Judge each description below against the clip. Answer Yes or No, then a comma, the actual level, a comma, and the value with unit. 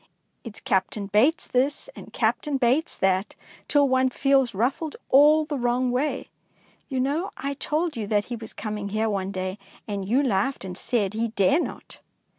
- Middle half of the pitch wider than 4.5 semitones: Yes, average, 5.1 semitones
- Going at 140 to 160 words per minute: No, average, 175 wpm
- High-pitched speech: Yes, high, 245 Hz